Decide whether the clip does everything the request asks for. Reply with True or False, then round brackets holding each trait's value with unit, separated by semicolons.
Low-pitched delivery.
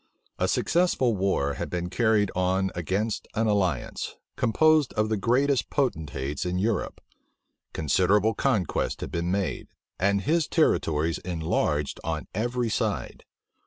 True (100 Hz)